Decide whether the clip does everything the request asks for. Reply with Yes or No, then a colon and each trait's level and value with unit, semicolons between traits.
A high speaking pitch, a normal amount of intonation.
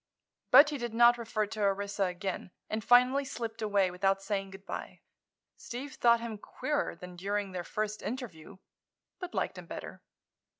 Yes: high, 215 Hz; average, 3.6 semitones